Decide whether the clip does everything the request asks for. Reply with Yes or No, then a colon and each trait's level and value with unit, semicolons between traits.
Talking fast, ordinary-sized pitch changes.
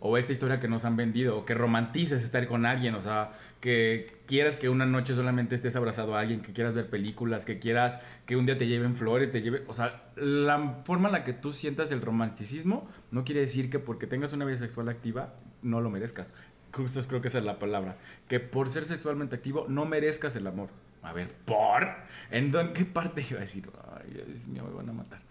Yes: fast, 225 wpm; average, 3.4 semitones